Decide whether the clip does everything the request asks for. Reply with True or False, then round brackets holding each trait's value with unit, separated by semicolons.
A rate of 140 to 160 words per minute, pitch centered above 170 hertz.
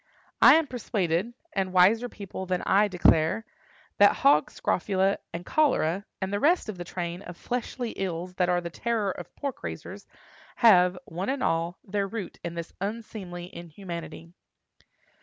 True (150 wpm; 190 Hz)